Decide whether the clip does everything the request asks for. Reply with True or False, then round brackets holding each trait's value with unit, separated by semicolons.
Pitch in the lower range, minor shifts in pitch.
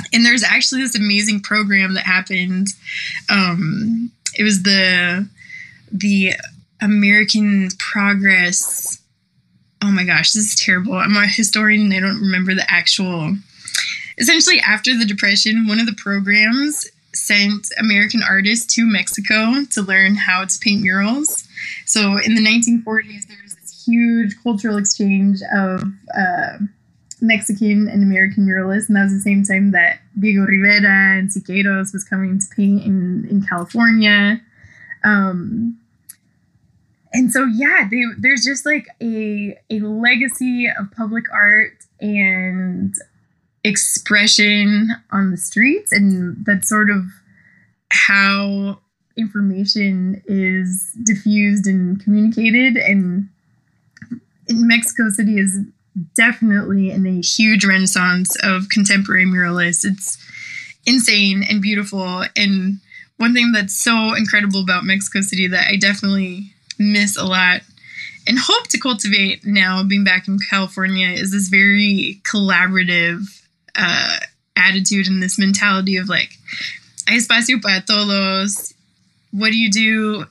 False (205 Hz; 2.3 semitones)